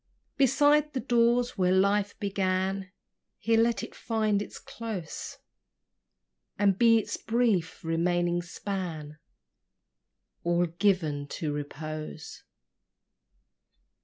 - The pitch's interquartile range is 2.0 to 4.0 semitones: No, average, 5.1 semitones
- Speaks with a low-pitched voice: No, high, 195 Hz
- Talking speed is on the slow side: Yes, slow, 95 wpm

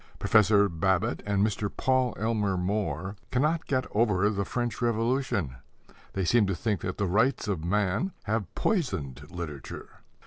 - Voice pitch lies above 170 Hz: No, low, 105 Hz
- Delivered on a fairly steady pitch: No, average, 4.2 semitones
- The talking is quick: No, average, 145 wpm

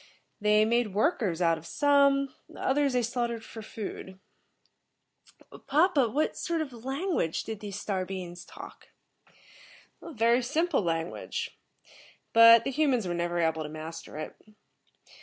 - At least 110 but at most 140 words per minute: Yes, slow, 135 wpm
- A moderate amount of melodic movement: No, wide, 7.3 semitones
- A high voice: Yes, high, 230 Hz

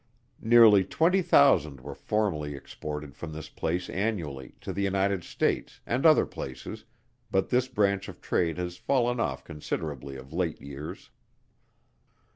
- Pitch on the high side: No, very low, 90 Hz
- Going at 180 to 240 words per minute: No, average, 140 wpm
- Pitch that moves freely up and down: Yes, wide, 6.4 semitones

